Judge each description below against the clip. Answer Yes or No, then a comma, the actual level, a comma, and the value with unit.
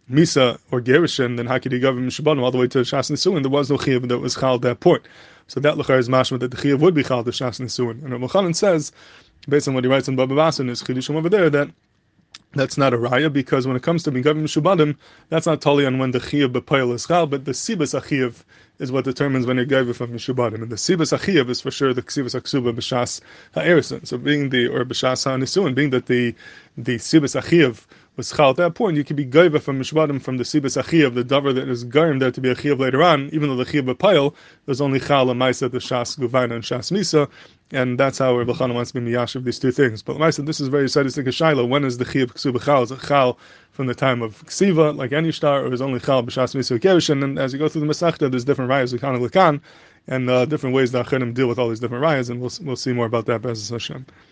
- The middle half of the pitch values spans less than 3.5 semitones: Yes, average, 2.8 semitones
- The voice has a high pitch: No, low, 130 Hz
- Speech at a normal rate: No, fast, 245 wpm